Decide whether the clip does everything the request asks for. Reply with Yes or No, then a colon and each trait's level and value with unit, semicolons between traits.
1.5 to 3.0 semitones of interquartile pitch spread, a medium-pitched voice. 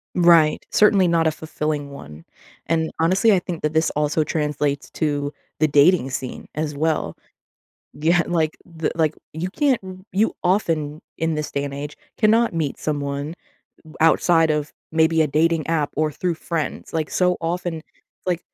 Yes: narrow, 2.4 semitones; medium, 160 Hz